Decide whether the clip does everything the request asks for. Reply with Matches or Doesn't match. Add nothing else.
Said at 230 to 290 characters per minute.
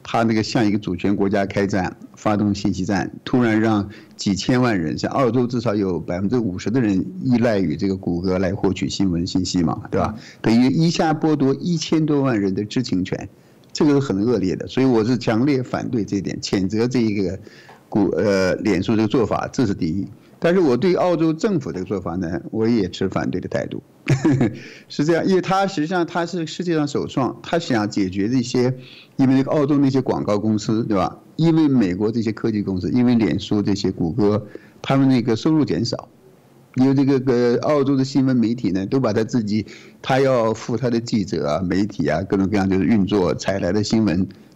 Doesn't match